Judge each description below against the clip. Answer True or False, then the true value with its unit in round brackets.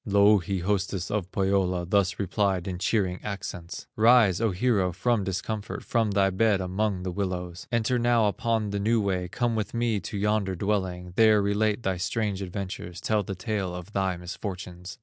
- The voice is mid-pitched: False (100 Hz)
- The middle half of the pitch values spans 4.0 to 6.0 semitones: False (2.7 semitones)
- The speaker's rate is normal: True (170 wpm)